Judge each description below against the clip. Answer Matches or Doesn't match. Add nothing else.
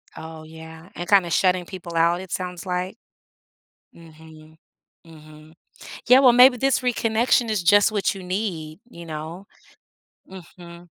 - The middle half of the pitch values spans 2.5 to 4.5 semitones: Matches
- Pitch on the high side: Doesn't match